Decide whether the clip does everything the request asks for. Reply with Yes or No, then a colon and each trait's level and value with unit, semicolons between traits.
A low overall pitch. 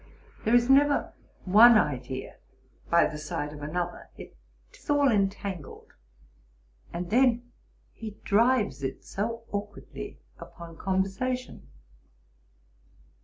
No: high, 205 Hz